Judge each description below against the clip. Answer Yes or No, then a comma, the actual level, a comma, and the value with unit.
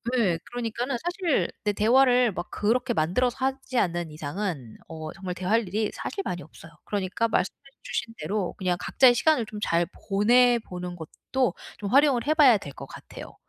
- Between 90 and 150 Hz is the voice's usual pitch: No, high, 210 Hz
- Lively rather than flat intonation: Yes, wide, 5.8 semitones